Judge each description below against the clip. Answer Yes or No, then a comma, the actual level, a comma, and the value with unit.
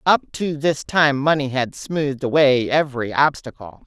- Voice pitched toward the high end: No, medium, 140 Hz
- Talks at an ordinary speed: Yes, average, 155 wpm